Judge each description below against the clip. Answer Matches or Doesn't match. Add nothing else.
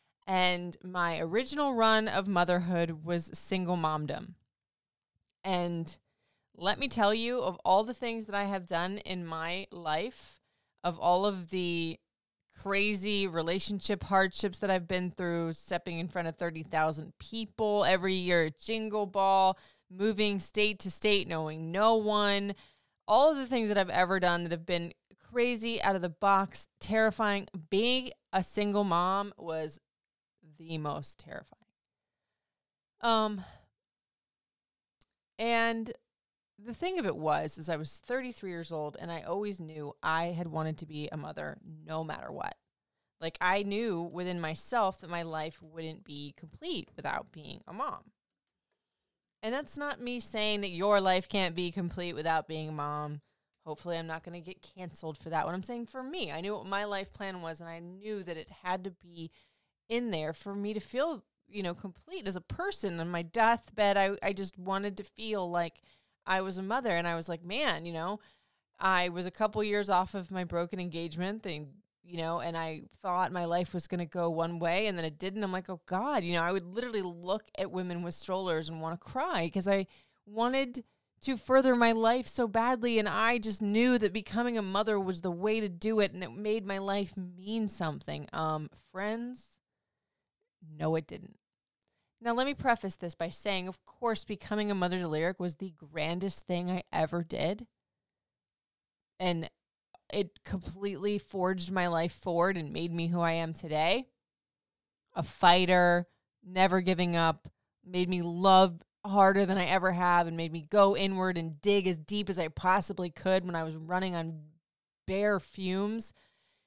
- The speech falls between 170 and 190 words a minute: Matches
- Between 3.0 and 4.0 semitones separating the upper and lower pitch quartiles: Matches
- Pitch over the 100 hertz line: Matches